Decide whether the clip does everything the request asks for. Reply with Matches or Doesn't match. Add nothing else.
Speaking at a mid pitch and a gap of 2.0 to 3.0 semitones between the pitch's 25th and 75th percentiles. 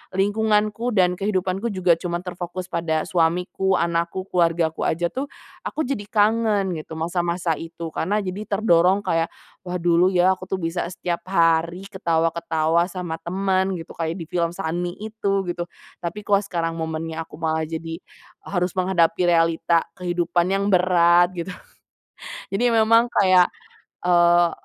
Matches